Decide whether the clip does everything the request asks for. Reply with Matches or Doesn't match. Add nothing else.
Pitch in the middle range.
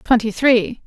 Doesn't match